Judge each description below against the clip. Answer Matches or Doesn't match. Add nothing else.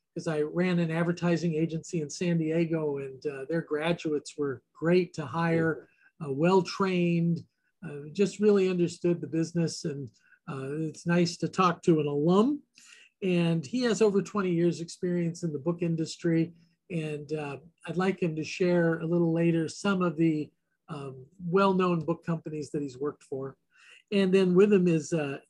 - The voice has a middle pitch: Matches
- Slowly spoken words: Doesn't match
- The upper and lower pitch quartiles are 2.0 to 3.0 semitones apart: Matches